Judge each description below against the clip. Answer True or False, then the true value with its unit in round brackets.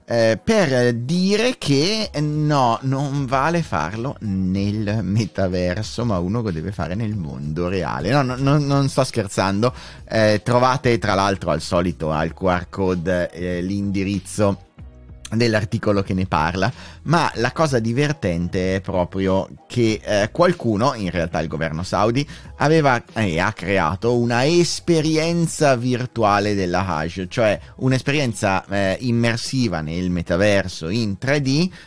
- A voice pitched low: True (105 Hz)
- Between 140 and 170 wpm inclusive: False (130 wpm)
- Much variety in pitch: True (6.0 semitones)